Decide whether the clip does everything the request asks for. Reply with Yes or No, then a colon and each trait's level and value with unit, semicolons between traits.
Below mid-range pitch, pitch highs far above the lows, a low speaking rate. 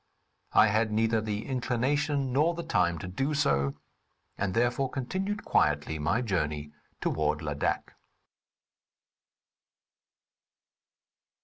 Yes: low, 110 Hz; wide, 9.0 semitones; slow, 100 wpm